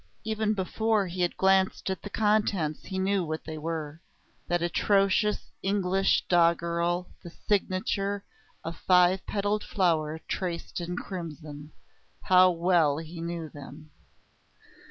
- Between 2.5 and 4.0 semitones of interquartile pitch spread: Yes, average, 2.9 semitones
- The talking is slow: Yes, slow, 125 wpm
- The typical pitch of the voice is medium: Yes, medium, 180 Hz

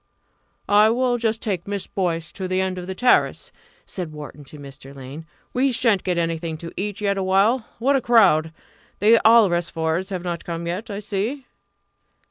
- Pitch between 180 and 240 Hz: Yes, high, 190 Hz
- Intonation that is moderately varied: Yes, average, 4.8 semitones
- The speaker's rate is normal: Yes, average, 170 wpm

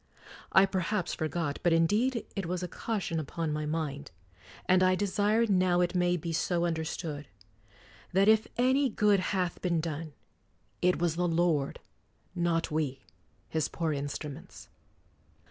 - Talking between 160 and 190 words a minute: No, average, 145 wpm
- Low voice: No, medium, 175 Hz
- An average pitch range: Yes, average, 3.1 semitones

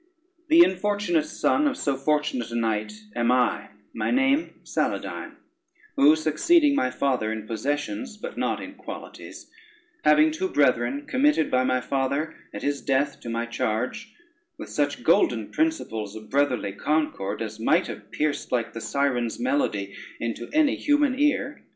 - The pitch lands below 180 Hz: Yes, medium, 140 Hz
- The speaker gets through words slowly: No, average, 150 wpm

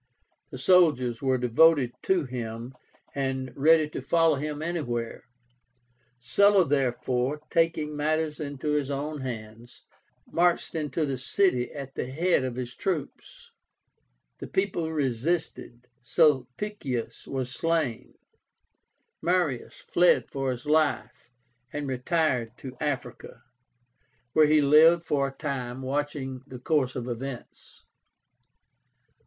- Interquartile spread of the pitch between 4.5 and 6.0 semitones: No, average, 3.9 semitones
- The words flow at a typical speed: No, slow, 115 wpm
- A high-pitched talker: No, medium, 140 Hz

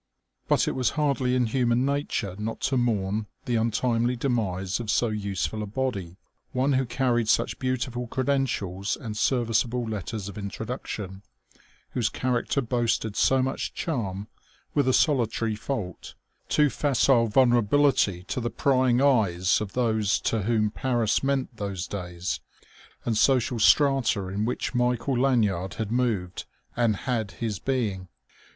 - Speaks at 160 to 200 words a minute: No, average, 140 wpm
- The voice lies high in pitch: No, low, 115 Hz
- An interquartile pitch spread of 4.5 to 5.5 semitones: No, average, 3.8 semitones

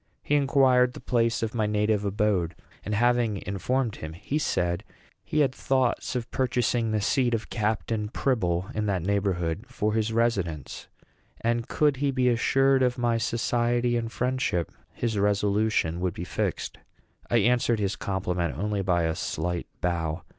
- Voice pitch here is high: No, low, 110 Hz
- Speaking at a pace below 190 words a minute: Yes, average, 160 wpm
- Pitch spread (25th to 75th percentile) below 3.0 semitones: No, average, 4.2 semitones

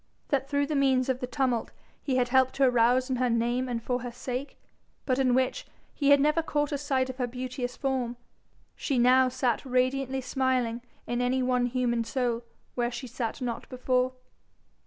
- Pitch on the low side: No, very high, 255 Hz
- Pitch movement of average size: No, narrow, 1.3 semitones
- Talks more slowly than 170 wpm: No, average, 185 wpm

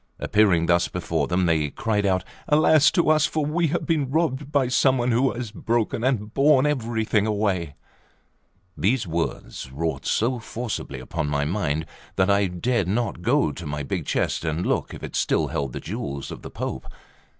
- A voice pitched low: Yes, low, 105 Hz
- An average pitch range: No, wide, 7.6 semitones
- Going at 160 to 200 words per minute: Yes, average, 185 wpm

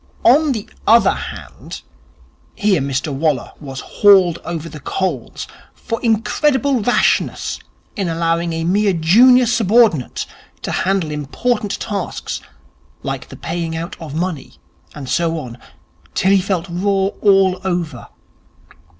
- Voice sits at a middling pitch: Yes, medium, 180 Hz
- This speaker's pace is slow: Yes, slow, 125 wpm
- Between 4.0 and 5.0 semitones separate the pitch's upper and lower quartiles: Yes, average, 4.3 semitones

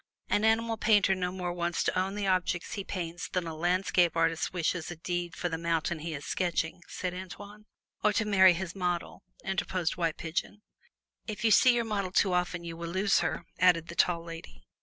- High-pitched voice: No, medium, 180 Hz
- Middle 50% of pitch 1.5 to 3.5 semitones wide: Yes, narrow, 2.4 semitones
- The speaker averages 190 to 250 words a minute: Yes, average, 200 wpm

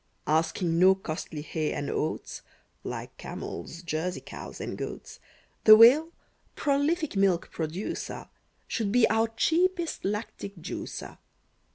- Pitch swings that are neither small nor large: No, wide, 6.9 semitones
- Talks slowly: Yes, slow, 115 wpm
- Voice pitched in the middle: No, high, 195 Hz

